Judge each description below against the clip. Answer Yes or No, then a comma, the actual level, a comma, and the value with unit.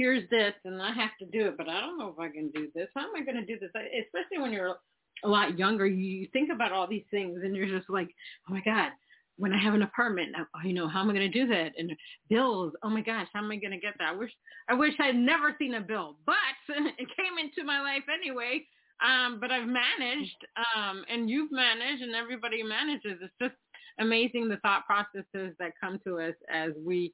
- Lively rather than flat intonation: No, average, 4.9 semitones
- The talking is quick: Yes, fast, 250 wpm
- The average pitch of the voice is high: Yes, high, 215 Hz